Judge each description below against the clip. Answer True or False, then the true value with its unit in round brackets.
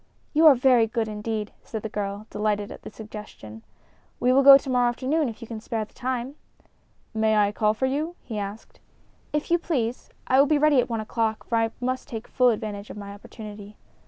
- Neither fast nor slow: False (215 wpm)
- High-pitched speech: True (225 Hz)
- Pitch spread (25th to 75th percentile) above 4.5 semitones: False (3.5 semitones)